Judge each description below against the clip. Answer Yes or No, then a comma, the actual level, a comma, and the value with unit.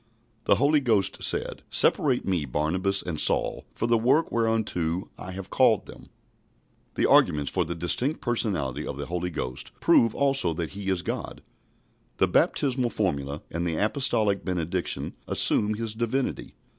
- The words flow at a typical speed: Yes, average, 155 wpm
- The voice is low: Yes, very low, 95 Hz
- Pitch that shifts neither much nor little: No, wide, 5.7 semitones